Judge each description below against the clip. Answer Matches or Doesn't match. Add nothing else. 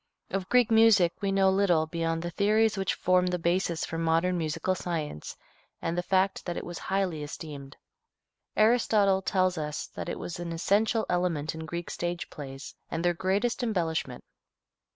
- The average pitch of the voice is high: Doesn't match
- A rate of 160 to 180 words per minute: Matches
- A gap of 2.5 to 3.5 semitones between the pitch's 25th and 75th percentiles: Matches